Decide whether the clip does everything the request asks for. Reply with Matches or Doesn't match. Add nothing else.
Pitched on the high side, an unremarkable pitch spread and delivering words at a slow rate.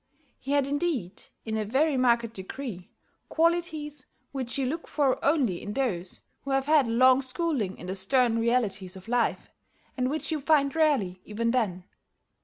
Doesn't match